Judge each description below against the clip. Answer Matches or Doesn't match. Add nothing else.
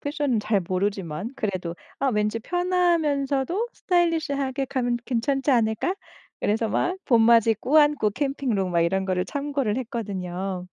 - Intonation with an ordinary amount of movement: Doesn't match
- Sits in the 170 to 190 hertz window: Doesn't match